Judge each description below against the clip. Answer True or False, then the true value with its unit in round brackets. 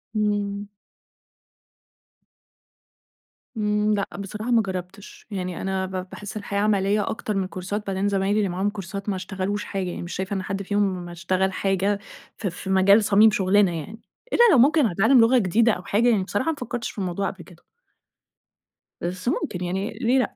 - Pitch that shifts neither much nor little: False (2.0 semitones)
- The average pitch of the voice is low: False (200 Hz)